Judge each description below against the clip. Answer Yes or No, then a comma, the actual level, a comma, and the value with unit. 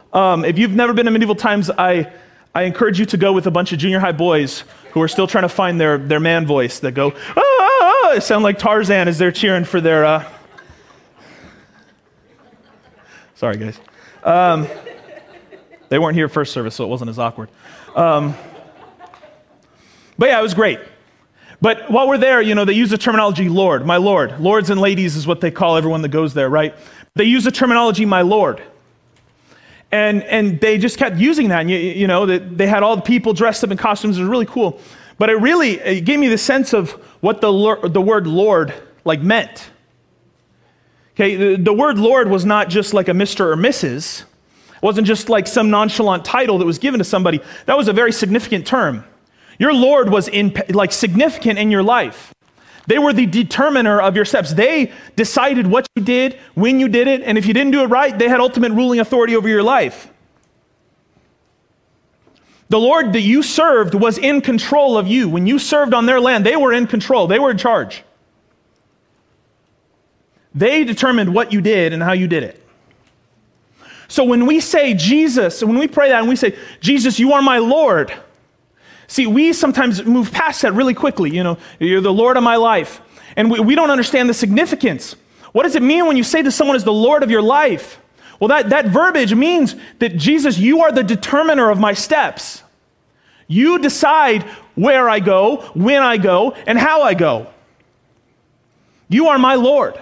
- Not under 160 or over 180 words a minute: No, average, 195 wpm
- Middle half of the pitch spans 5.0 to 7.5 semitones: Yes, average, 5.3 semitones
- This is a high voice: Yes, high, 220 Hz